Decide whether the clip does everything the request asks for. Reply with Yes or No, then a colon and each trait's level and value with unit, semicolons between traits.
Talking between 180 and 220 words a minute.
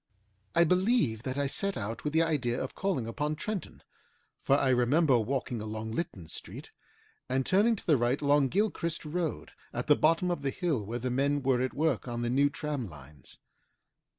Yes: average, 190 wpm